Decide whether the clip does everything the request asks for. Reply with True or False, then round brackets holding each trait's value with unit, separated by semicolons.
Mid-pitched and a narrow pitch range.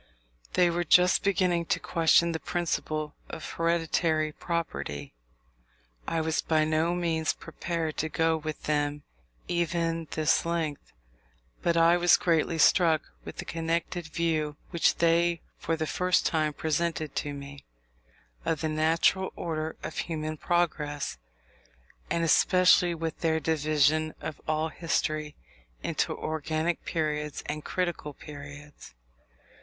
True (160 Hz; 1.6 semitones)